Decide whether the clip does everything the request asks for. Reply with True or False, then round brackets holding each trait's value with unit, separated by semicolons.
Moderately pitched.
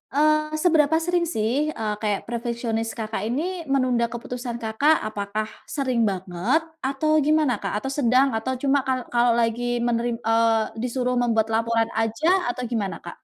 False (240 Hz)